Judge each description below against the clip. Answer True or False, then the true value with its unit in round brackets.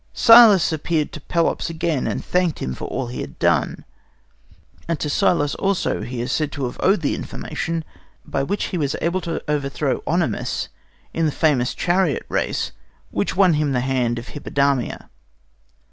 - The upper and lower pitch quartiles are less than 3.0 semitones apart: False (4.2 semitones)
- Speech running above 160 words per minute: True (170 wpm)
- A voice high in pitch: False (150 Hz)